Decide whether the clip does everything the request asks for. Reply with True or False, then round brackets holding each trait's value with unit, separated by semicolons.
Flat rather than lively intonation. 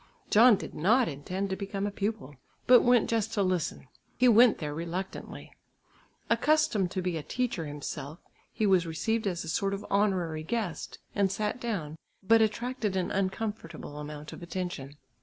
False (5.0 semitones)